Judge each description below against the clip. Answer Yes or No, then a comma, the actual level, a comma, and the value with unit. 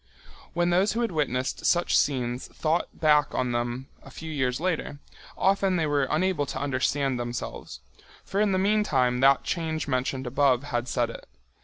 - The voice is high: No, medium, 145 Hz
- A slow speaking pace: No, average, 170 wpm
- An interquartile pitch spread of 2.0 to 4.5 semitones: No, average, 5.2 semitones